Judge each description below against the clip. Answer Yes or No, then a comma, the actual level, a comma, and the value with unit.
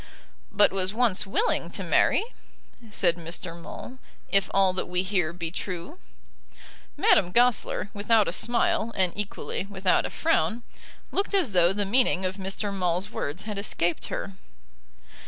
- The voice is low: No, high, 195 Hz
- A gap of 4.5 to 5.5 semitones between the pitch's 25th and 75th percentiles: No, average, 3.2 semitones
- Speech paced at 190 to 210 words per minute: No, average, 150 wpm